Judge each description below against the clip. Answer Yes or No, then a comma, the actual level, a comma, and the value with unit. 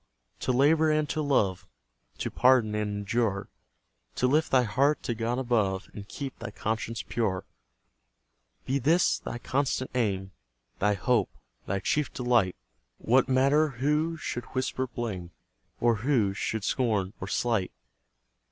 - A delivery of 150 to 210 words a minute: No, average, 140 wpm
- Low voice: Yes, low, 120 Hz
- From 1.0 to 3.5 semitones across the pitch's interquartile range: No, average, 4.3 semitones